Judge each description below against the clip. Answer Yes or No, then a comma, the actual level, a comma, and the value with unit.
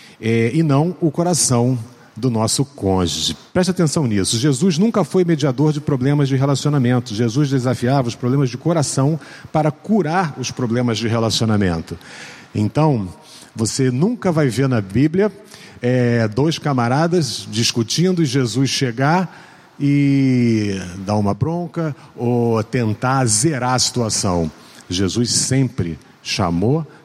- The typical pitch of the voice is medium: No, low, 130 Hz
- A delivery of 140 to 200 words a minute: No, average, 125 wpm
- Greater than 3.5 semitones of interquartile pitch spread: Yes, average, 5.2 semitones